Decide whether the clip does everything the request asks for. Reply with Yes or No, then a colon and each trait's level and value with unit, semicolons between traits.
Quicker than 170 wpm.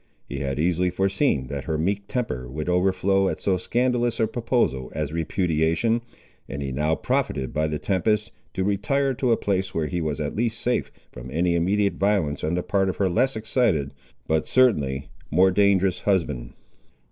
Yes: average, 180 wpm